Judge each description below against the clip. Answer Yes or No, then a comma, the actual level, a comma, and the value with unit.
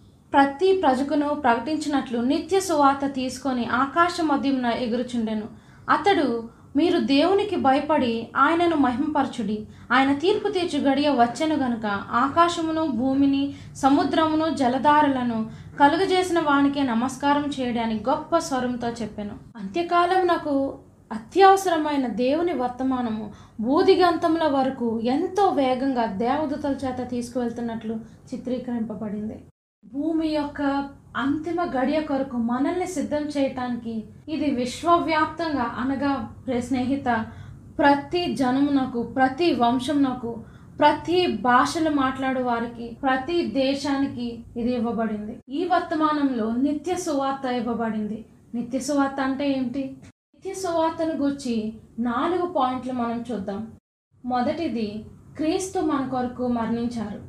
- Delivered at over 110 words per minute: No, average, 95 wpm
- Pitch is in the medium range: No, very high, 270 Hz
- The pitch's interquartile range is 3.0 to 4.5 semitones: Yes, average, 4.2 semitones